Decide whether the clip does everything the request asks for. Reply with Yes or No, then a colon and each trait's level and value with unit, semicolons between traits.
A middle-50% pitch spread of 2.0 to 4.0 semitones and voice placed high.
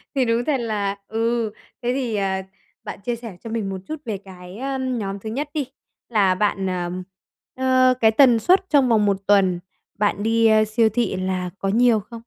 Yes: average, 3.7 semitones; high, 220 Hz